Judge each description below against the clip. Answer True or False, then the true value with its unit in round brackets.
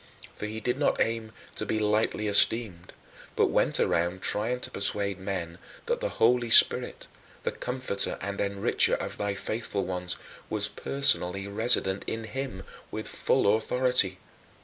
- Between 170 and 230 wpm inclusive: False (150 wpm)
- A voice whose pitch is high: False (105 Hz)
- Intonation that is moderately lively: True (3.3 semitones)